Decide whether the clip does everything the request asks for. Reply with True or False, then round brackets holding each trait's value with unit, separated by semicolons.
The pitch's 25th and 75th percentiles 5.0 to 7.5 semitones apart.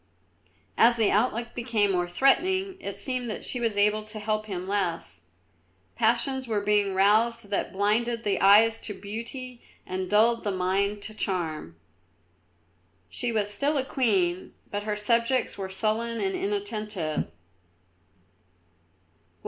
False (3.0 semitones)